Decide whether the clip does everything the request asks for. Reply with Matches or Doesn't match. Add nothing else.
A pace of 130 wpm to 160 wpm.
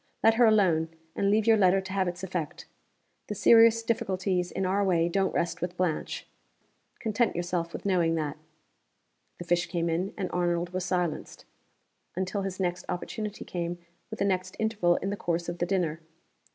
Doesn't match